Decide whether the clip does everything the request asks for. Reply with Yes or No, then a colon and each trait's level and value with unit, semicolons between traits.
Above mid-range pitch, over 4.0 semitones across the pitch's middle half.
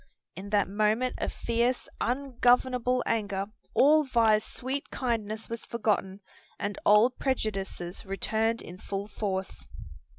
No: high, 220 Hz; average, 3.5 semitones